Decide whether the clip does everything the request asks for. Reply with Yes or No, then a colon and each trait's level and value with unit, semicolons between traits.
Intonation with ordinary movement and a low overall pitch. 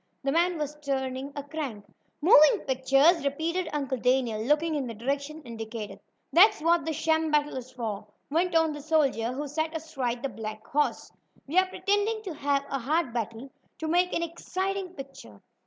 No: average, 4.0 semitones; very high, 290 Hz